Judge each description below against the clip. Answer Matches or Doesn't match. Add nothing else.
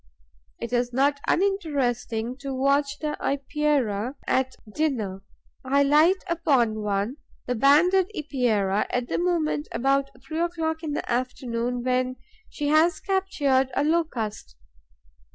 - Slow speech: Matches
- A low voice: Doesn't match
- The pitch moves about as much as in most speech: Matches